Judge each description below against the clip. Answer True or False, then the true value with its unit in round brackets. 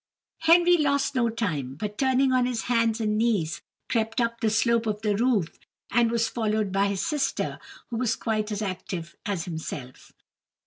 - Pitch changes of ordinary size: True (3.2 semitones)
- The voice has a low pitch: False (225 Hz)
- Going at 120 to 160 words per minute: False (175 wpm)